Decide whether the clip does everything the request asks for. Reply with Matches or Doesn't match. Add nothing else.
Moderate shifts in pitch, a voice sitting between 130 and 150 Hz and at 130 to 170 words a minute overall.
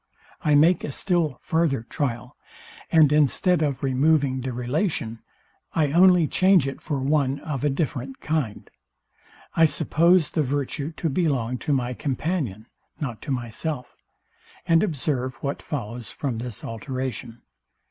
Matches